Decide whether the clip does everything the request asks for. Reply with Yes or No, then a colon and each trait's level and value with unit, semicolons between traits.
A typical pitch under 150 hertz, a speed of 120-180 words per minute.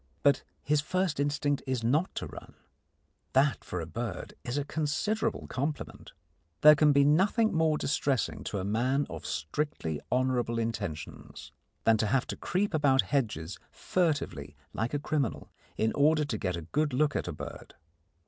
Yes: medium, 140 Hz; average, 165 wpm